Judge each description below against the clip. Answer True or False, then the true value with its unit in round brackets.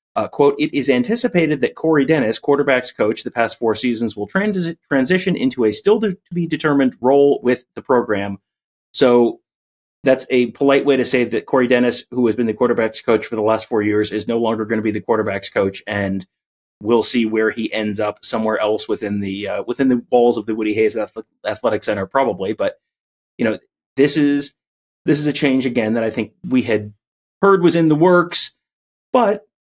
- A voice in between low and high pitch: False (125 Hz)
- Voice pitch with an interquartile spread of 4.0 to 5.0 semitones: True (4.6 semitones)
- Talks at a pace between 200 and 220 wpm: True (205 wpm)